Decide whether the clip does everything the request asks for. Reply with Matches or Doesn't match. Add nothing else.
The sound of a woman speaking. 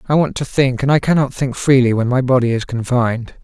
Doesn't match